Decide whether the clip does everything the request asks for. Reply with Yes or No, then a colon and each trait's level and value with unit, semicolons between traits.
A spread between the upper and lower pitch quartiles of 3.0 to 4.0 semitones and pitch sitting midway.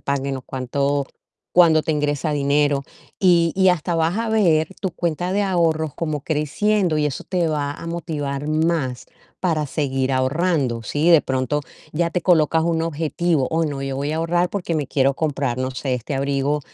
Yes: average, 3.4 semitones; medium, 150 Hz